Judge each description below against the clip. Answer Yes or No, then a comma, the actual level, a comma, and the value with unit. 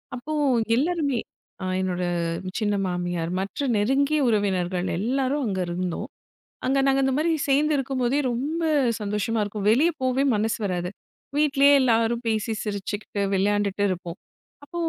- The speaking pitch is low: No, high, 225 Hz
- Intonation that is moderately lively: No, wide, 5.8 semitones